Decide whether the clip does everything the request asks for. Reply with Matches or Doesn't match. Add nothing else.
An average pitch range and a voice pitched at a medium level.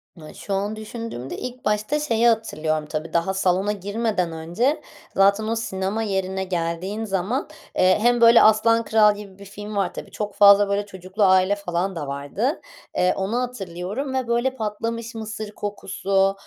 Doesn't match